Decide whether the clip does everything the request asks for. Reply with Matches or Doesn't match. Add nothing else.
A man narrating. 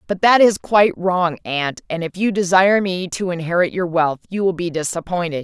Doesn't match